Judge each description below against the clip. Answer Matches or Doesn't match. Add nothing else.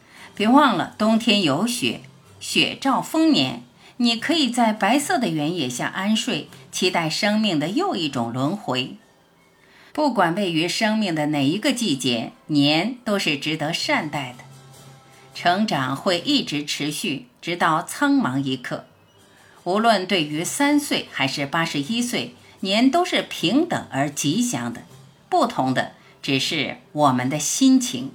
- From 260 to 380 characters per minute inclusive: Doesn't match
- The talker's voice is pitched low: Doesn't match